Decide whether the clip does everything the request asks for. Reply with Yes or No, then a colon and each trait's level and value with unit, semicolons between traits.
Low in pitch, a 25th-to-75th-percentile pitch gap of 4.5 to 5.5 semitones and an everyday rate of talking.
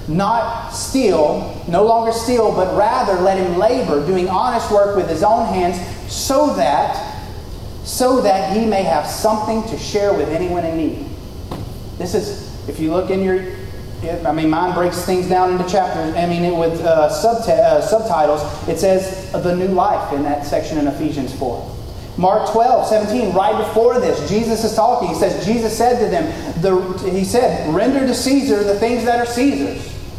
No: high, 190 Hz; average, 5.2 semitones; average, 180 wpm